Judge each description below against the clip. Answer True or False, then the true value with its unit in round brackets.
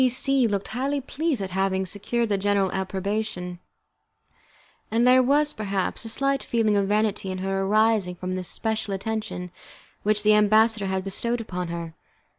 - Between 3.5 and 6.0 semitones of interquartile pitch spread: False (3.1 semitones)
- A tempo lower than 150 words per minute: False (165 wpm)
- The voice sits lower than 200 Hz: False (210 Hz)